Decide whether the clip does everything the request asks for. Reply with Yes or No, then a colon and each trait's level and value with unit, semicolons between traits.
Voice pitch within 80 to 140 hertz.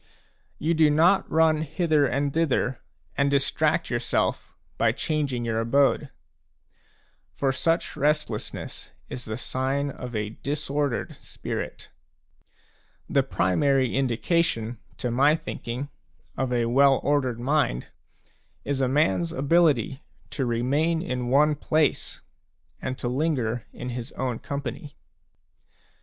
Yes: low, 135 Hz